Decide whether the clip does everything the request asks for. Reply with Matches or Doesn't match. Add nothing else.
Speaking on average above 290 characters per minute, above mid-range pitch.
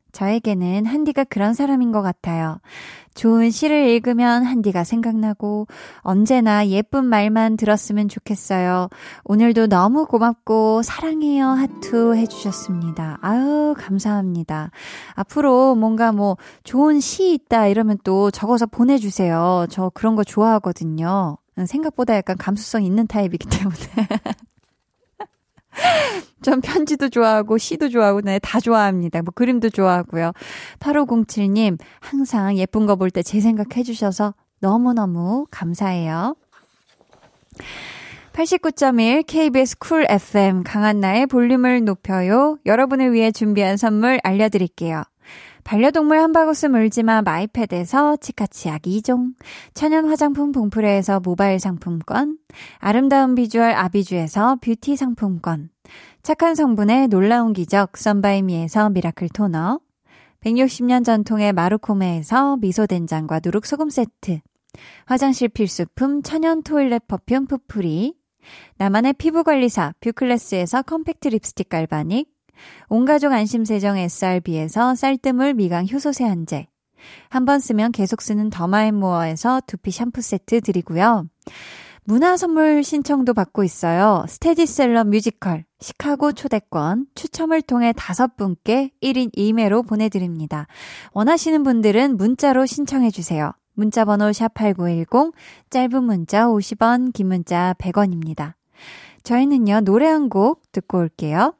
Doesn't match